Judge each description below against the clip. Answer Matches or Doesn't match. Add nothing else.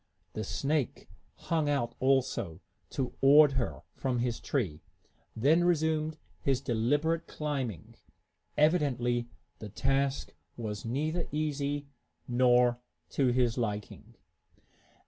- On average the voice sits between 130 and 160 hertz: Matches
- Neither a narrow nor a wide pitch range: Matches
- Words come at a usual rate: Doesn't match